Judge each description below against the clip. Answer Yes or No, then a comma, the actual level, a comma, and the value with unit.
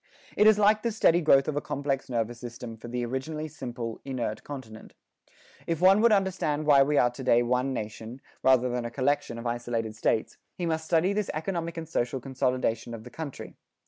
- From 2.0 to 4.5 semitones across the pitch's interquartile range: No, average, 5.1 semitones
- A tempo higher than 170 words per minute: Yes, average, 200 wpm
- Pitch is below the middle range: Yes, low, 130 Hz